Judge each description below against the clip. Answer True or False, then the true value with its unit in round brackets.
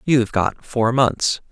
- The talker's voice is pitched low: True (120 Hz)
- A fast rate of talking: False (160 wpm)